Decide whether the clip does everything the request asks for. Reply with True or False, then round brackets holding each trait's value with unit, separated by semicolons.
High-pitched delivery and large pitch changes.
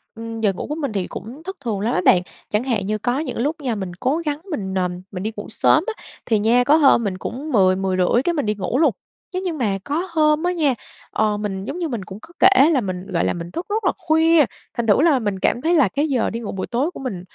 True (240 Hz; 7.3 semitones)